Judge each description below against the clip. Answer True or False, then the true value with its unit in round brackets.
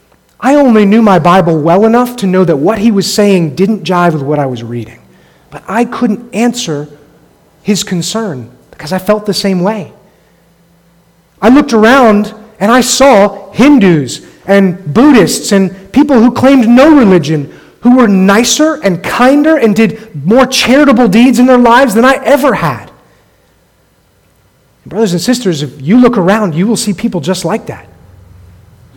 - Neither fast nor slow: True (165 wpm)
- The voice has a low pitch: False (205 Hz)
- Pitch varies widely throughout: True (5.8 semitones)